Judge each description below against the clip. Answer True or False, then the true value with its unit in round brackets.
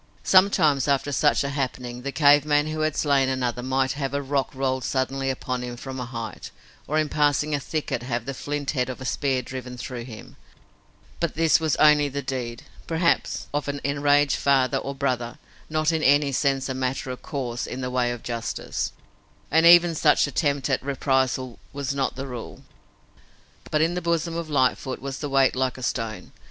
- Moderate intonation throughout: False (2.3 semitones)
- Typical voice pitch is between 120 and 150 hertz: True (135 Hz)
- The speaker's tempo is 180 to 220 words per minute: True (195 wpm)